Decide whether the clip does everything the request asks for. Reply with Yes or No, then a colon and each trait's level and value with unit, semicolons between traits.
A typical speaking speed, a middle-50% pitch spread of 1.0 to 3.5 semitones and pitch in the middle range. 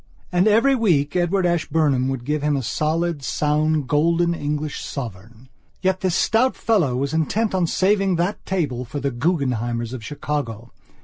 No: average, 160 wpm; average, 5.1 semitones; medium, 150 Hz